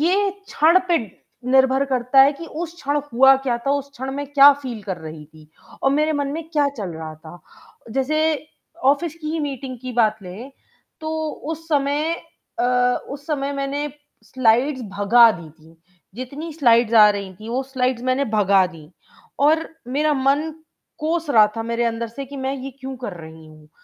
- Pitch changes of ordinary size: Yes, average, 4.5 semitones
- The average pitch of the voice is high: Yes, very high, 265 Hz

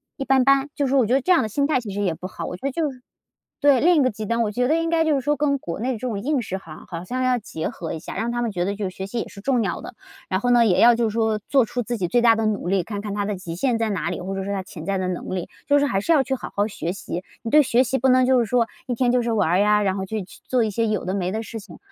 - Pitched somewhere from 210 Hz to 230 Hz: Yes, high, 225 Hz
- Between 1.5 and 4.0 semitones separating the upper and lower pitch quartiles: No, average, 4.6 semitones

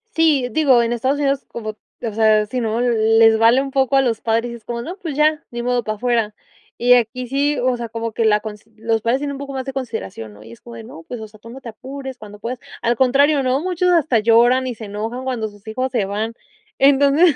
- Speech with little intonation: No, average, 3.5 semitones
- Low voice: No, high, 240 Hz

